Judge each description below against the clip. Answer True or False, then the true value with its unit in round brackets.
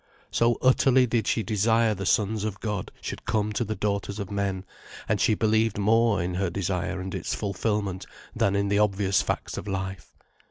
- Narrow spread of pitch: True (2.2 semitones)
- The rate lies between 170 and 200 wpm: True (190 wpm)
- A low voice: True (100 Hz)